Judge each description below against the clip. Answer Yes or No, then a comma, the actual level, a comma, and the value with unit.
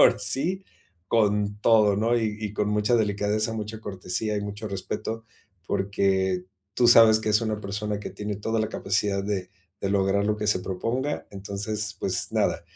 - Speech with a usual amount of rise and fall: No, narrow, 1.7 semitones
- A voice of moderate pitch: No, low, 105 Hz